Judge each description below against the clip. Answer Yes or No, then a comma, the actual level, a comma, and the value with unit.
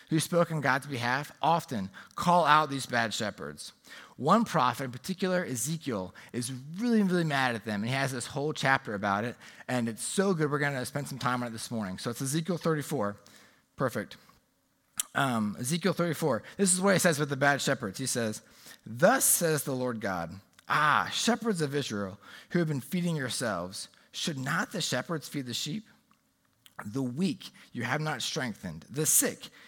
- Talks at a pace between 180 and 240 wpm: Yes, average, 185 wpm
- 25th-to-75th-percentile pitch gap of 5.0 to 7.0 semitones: Yes, wide, 5.5 semitones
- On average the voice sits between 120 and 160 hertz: Yes, medium, 140 Hz